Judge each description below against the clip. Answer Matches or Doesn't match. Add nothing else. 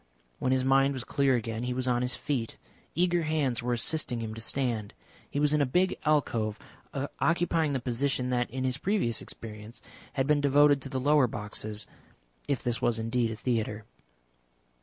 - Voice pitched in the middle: Doesn't match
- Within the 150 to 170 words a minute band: Doesn't match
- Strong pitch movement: Doesn't match